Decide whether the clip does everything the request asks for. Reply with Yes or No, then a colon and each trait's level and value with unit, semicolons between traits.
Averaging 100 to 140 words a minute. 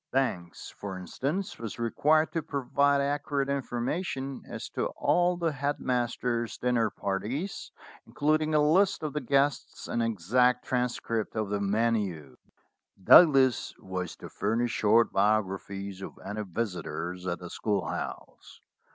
Yes: slow, 135 wpm